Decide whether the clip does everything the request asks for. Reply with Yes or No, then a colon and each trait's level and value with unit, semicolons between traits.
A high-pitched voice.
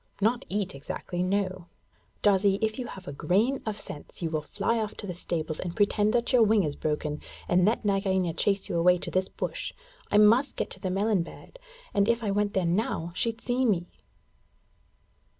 Yes: high, 195 Hz